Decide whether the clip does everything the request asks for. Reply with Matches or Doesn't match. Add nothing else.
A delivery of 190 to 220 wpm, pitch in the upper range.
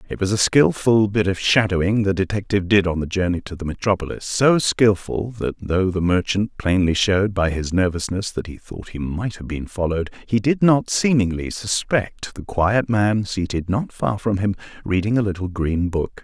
Doesn't match